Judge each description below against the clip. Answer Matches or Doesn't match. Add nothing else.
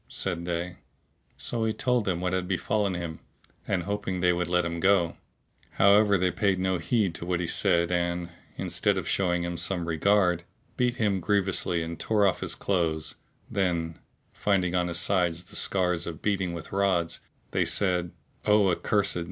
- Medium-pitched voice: Doesn't match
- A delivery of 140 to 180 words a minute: Matches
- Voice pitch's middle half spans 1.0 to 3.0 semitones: Matches